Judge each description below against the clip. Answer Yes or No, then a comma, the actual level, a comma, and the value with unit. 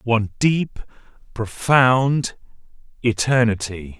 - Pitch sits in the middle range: No, low, 115 Hz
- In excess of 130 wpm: No, slow, 60 wpm